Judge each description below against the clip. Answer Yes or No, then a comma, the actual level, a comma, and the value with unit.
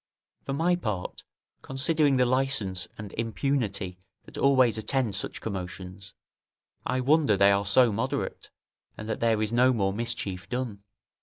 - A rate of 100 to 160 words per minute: Yes, average, 145 wpm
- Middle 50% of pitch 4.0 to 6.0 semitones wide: Yes, average, 5.0 semitones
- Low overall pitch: Yes, low, 115 Hz